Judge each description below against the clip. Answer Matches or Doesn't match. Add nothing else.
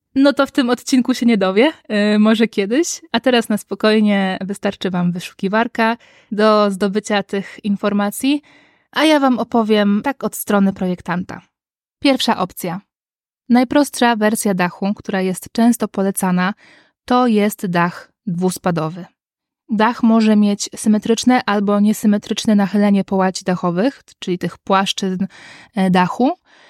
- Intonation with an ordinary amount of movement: Matches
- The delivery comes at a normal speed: Matches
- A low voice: Doesn't match